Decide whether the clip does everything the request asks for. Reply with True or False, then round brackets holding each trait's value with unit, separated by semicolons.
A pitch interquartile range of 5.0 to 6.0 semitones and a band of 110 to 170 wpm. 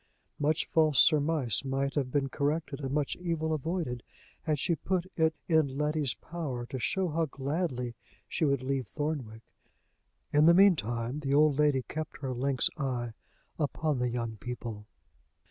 False (3.6 semitones; 160 wpm)